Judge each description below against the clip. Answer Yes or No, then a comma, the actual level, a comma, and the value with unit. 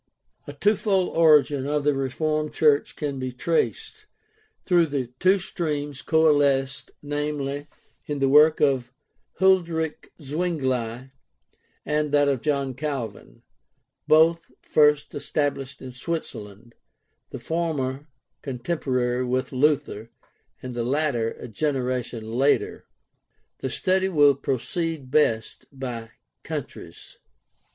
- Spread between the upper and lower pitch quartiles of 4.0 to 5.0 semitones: No, average, 3.1 semitones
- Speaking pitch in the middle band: Yes, medium, 145 Hz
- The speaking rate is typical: No, slow, 110 wpm